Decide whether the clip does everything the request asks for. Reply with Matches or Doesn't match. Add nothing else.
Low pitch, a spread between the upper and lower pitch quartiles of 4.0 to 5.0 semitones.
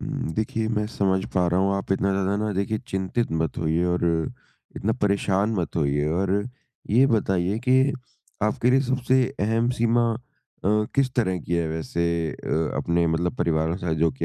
Matches